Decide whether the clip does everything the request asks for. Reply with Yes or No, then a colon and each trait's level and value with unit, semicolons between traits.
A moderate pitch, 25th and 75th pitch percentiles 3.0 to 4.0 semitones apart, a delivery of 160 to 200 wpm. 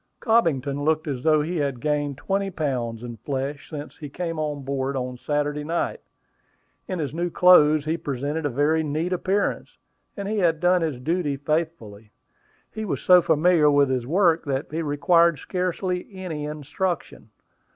Yes: medium, 155 Hz; average, 3.5 semitones; average, 165 wpm